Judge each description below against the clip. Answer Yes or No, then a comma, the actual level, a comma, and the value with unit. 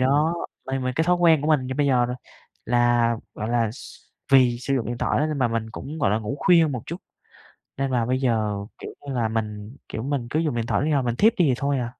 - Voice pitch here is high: No, low, 130 Hz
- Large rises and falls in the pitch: No, average, 3.5 semitones